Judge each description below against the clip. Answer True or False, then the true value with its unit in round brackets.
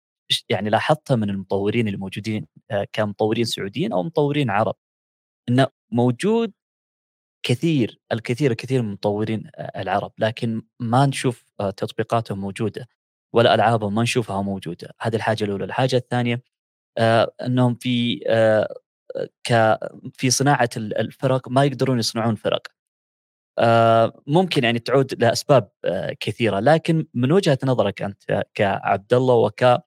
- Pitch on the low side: True (120 Hz)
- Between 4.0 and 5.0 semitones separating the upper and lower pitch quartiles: False (3.5 semitones)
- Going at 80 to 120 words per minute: True (110 wpm)